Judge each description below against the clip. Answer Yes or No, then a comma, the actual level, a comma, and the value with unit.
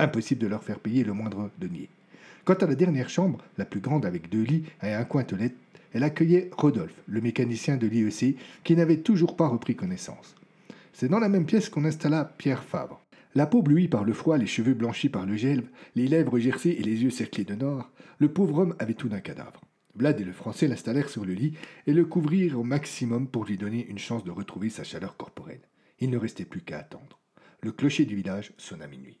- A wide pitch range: Yes, wide, 6.4 semitones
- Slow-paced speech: No, fast, 220 wpm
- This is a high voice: No, low, 135 Hz